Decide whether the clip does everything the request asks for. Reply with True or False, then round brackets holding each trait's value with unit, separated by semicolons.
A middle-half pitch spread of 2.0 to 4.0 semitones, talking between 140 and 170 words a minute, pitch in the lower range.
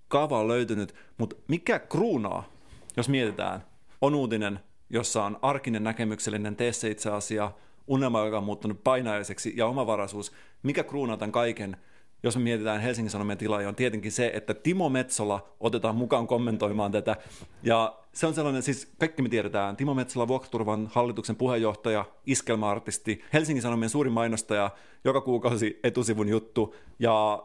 True (2.8 semitones; 150 wpm; 110 Hz)